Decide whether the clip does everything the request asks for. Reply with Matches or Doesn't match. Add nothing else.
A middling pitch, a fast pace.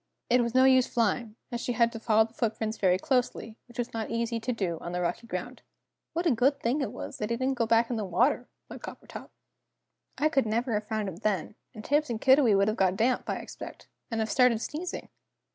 Doesn't match